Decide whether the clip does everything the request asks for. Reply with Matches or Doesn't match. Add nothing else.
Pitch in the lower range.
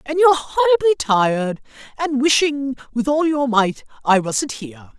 Doesn't match